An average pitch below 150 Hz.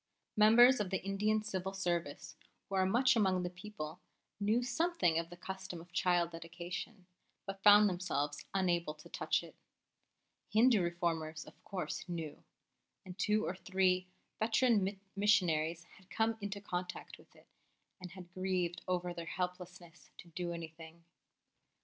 No: medium, 185 Hz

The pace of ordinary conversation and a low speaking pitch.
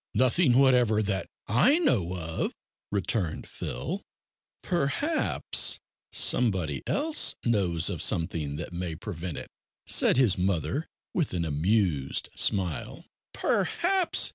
No: slow, 110 wpm; low, 100 Hz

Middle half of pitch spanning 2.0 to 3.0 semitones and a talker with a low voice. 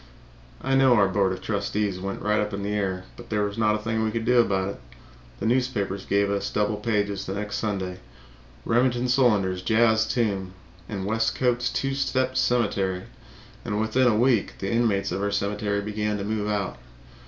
Yes: narrow, 2.6 semitones; low, 105 Hz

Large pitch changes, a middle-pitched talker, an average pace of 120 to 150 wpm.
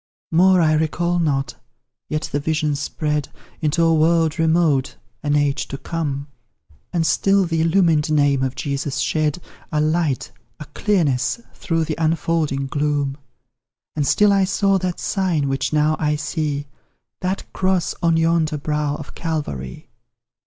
No: narrow, 2.6 semitones; medium, 155 Hz; average, 145 wpm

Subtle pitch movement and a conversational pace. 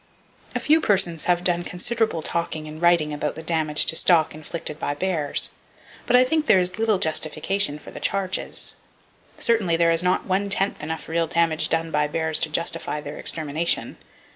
No: average, 3.1 semitones; average, 180 wpm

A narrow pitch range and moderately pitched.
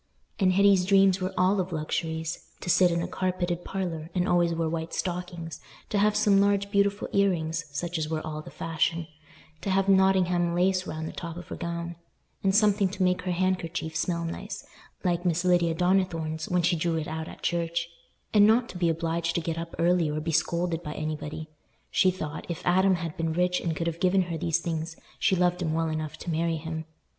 Yes: narrow, 2.2 semitones; medium, 170 Hz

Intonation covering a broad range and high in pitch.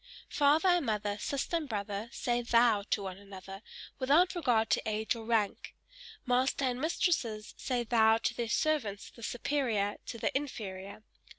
No: average, 4.5 semitones; high, 230 Hz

